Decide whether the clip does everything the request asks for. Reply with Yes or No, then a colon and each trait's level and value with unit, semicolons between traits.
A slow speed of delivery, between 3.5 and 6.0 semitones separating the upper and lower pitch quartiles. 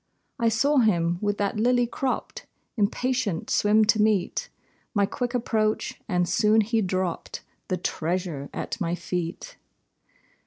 Yes: slow, 130 wpm; average, 4.3 semitones